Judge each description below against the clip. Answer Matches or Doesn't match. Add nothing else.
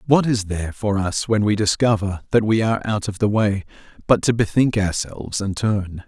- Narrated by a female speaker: Doesn't match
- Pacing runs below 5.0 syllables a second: Doesn't match